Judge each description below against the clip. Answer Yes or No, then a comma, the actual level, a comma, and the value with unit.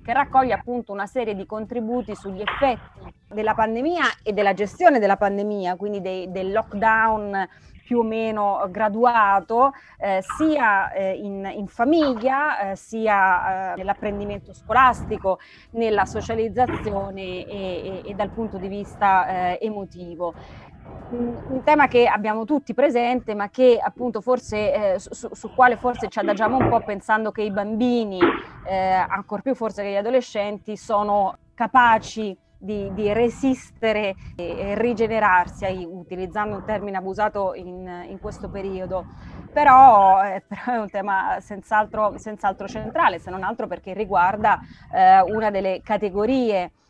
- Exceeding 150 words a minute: No, average, 145 wpm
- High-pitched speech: Yes, high, 210 Hz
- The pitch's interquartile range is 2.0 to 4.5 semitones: Yes, average, 3.2 semitones